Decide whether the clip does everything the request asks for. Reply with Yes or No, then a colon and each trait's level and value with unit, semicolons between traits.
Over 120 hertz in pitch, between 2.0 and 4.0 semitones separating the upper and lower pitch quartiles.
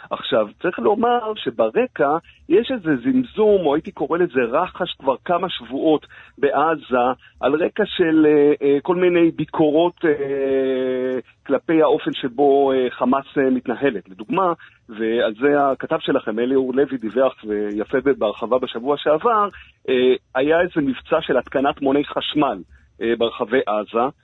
No: medium, 140 Hz; average, 4.7 semitones